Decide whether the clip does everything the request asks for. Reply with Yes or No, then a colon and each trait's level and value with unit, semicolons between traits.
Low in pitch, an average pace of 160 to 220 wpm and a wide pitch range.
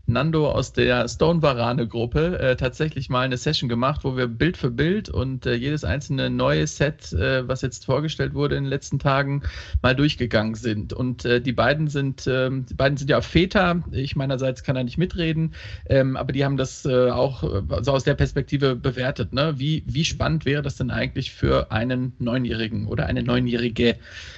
No: low, 130 Hz; fast, 190 wpm; average, 2.8 semitones